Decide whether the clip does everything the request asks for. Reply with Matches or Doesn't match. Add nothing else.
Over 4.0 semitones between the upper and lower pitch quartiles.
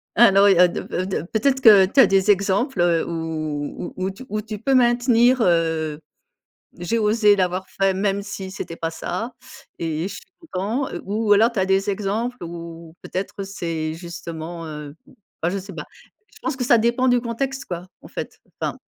Matches